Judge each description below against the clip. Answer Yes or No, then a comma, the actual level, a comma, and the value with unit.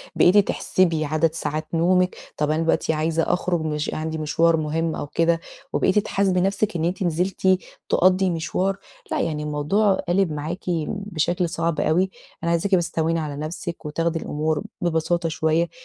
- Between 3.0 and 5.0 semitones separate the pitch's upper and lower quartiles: No, narrow, 2.6 semitones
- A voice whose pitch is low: No, medium, 165 Hz